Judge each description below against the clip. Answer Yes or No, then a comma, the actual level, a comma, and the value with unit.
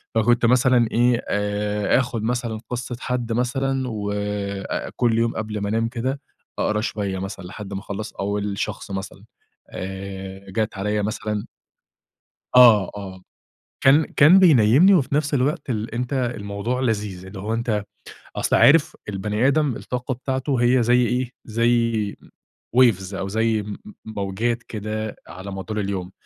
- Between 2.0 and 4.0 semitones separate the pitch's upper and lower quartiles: Yes, average, 3.4 semitones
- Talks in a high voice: No, low, 110 Hz